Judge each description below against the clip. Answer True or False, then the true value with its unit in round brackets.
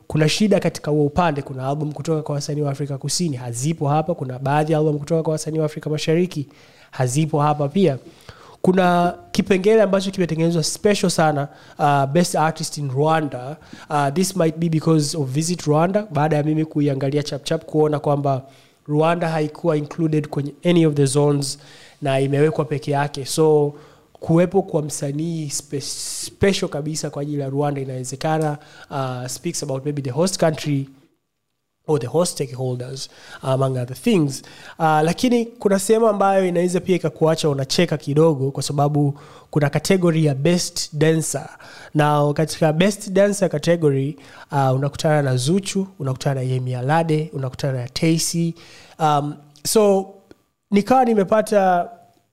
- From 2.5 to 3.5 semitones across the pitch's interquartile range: True (2.8 semitones)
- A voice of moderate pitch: True (155 Hz)